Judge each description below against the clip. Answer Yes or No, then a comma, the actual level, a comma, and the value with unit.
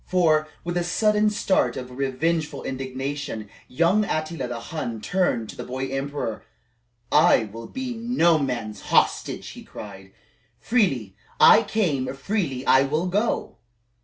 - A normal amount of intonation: No, wide, 6.1 semitones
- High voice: No, medium, 145 Hz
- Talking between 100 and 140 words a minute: Yes, slow, 135 wpm